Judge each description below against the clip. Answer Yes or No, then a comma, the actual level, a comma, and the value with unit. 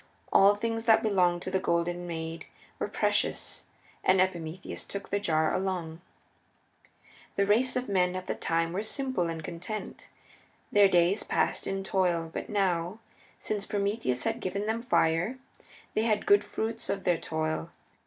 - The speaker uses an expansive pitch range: No, average, 3.8 semitones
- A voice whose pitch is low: No, high, 190 Hz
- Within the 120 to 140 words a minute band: No, average, 160 wpm